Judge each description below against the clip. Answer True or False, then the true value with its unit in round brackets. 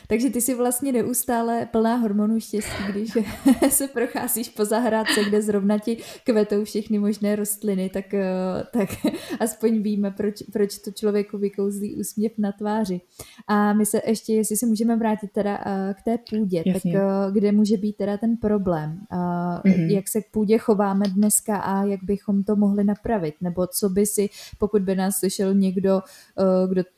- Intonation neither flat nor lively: False (2.0 semitones)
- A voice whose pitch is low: False (210 Hz)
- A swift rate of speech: False (160 wpm)